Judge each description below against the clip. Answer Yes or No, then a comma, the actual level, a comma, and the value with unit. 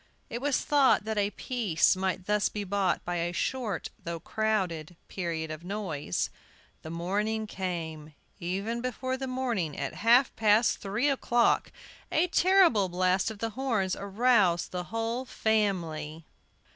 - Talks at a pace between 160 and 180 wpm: No, average, 145 wpm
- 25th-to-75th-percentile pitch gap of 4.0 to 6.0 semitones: Yes, average, 5.1 semitones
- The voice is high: Yes, high, 205 Hz